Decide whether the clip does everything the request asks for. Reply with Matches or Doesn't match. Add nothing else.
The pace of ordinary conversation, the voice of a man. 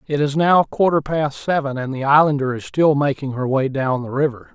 Doesn't match